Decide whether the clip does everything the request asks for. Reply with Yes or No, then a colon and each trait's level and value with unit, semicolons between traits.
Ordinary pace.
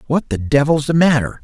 No: fast, 210 wpm